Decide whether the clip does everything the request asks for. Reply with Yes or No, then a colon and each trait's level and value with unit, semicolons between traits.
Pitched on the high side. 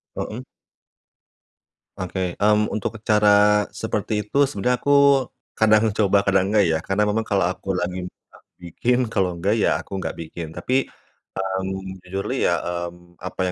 No: very low, 95 Hz